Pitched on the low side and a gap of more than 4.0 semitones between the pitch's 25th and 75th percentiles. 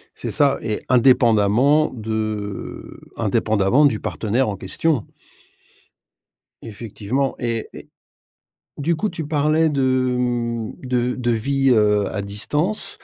Yes: low, 120 Hz; average, 4.4 semitones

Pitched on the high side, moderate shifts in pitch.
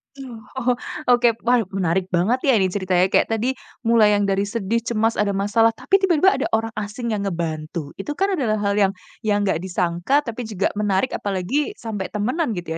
Yes: high, 210 Hz; average, 3.9 semitones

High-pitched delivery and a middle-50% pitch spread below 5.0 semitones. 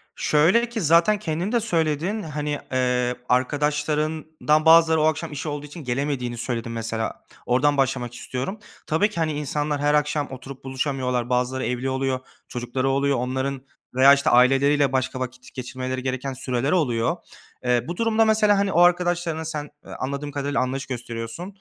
No: medium, 140 Hz; average, 3.8 semitones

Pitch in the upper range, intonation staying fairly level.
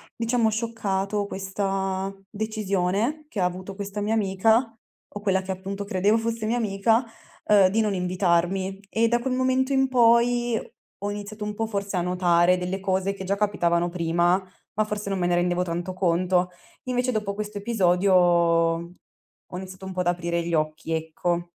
No: high, 195 Hz; average, 3.3 semitones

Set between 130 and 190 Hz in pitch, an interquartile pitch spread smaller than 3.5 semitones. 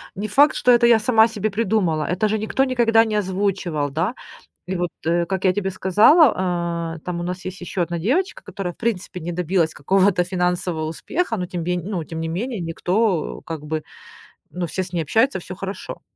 No: medium, 185 Hz; average, 3.9 semitones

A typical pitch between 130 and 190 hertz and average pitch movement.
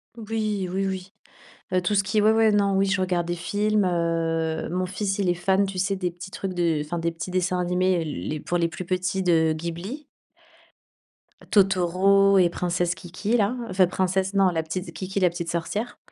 No: medium, 185 Hz; narrow, 2.3 semitones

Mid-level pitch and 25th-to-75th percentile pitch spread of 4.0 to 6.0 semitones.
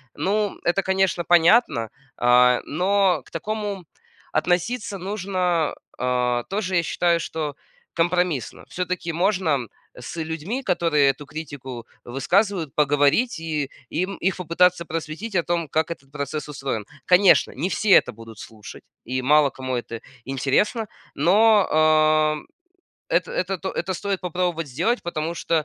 Yes: medium, 165 Hz; average, 4.6 semitones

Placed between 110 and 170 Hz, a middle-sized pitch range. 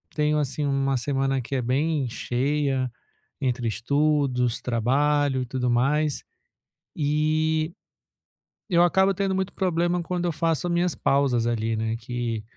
Yes: medium, 140 Hz; average, 4.1 semitones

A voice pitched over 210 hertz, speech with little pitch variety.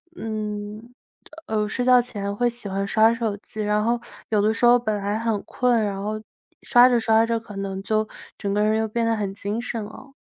Yes: high, 220 Hz; narrow, 2.1 semitones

